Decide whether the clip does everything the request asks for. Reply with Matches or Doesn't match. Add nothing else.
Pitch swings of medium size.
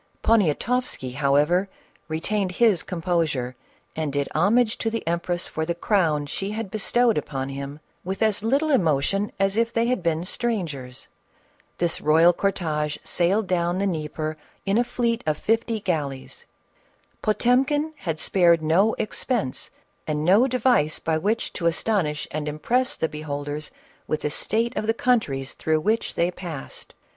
Doesn't match